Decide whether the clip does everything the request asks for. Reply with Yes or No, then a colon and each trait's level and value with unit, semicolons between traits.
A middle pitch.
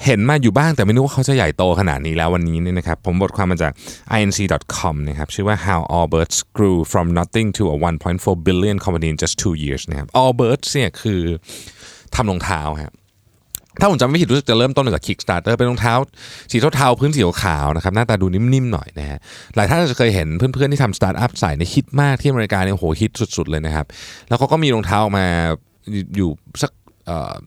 No: low, 100 Hz